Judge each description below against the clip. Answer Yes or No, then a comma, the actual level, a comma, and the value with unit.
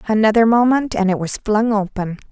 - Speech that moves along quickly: No, average, 180 wpm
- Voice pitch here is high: Yes, high, 215 Hz